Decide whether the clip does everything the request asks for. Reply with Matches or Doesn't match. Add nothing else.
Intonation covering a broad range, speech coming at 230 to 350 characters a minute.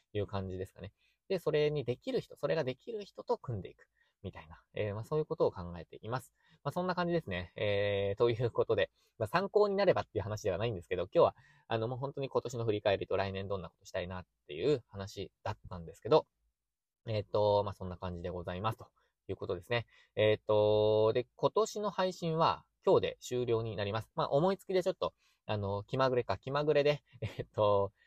Doesn't match